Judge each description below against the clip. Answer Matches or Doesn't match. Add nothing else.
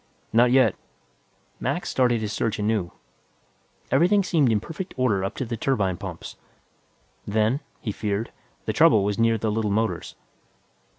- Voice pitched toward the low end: Matches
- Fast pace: Doesn't match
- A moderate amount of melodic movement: Matches